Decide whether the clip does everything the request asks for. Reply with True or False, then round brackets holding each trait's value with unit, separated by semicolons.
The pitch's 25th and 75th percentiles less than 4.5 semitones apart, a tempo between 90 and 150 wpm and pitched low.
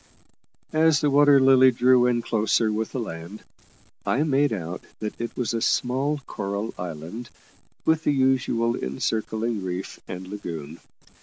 False (5.0 semitones; 145 wpm; 115 Hz)